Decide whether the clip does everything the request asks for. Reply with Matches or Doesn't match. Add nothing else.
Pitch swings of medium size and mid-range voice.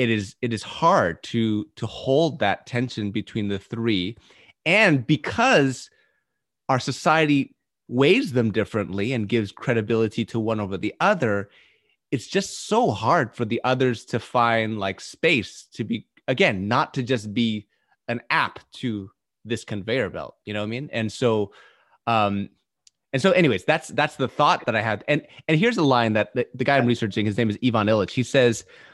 Doesn't match